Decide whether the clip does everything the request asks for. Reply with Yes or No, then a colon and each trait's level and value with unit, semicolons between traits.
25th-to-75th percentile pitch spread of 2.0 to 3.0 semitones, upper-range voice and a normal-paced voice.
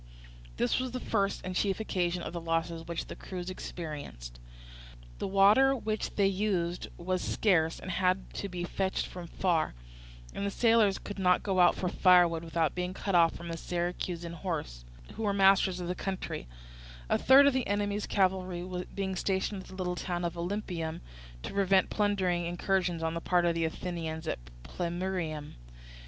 No: narrow, 2.4 semitones; medium, 180 Hz; average, 175 wpm